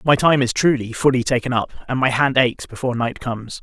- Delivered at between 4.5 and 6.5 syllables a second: Yes, 6.0 syllables/s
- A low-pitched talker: Yes, low, 125 Hz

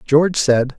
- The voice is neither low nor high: Yes, medium, 145 Hz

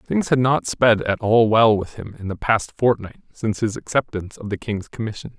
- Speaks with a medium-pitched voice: No, low, 110 Hz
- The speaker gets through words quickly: Yes, fast, 225 wpm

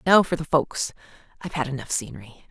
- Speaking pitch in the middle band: Yes, medium, 145 Hz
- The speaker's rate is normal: Yes, average, 170 wpm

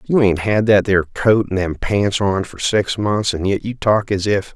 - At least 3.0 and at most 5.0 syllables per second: Yes, 4.5 syllables/s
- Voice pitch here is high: No, low, 100 Hz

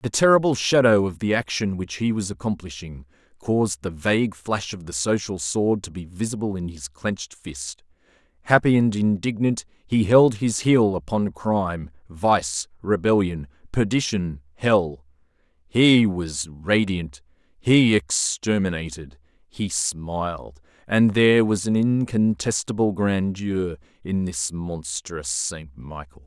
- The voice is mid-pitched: No, very low, 95 Hz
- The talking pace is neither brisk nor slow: No, slow, 130 wpm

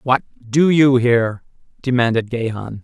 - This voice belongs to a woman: No, male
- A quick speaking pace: No, slow, 125 wpm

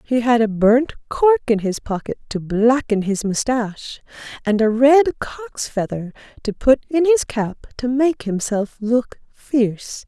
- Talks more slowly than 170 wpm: Yes, average, 160 wpm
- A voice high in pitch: Yes, high, 235 Hz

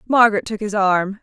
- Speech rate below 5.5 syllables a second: No, 5.7 syllables/s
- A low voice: No, high, 210 Hz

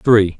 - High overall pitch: No, low, 110 Hz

